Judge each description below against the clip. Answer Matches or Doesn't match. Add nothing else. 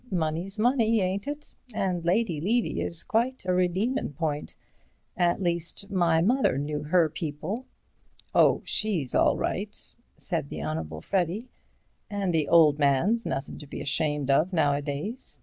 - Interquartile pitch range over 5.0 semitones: Matches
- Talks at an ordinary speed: Matches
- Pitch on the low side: Doesn't match